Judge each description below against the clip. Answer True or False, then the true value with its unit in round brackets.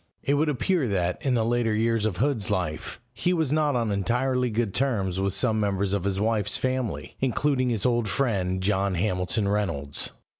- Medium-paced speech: True (185 wpm)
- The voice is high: False (110 Hz)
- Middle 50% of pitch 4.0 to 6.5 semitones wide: True (4.7 semitones)